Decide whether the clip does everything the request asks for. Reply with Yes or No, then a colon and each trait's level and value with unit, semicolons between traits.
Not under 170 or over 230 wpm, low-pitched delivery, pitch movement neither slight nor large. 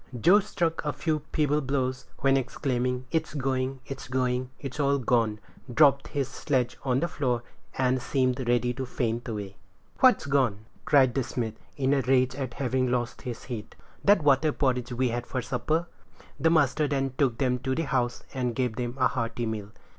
No: average, 185 wpm; low, 130 Hz; narrow, 2.2 semitones